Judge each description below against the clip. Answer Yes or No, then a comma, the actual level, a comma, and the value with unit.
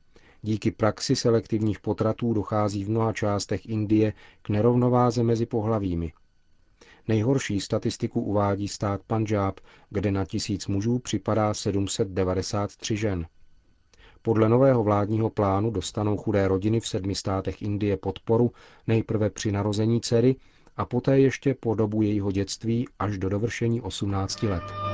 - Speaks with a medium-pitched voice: No, low, 105 Hz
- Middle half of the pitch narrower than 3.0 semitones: Yes, narrow, 2.5 semitones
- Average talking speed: Yes, average, 130 wpm